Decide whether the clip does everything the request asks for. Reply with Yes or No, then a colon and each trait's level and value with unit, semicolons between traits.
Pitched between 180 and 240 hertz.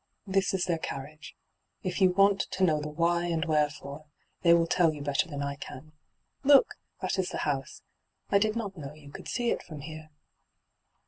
No: medium, 165 Hz